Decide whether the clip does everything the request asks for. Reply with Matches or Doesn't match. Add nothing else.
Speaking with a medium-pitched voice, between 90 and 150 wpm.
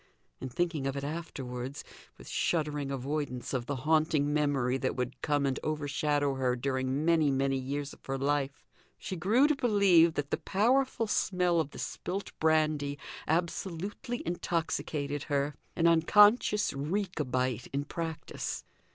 Matches